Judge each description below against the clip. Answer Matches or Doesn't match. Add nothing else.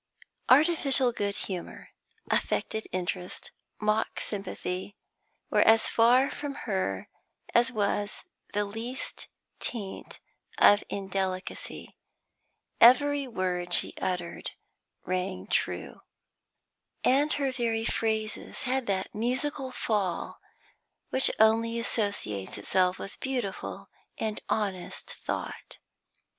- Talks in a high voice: Matches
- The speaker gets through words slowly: Matches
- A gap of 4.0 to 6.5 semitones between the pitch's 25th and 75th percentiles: Matches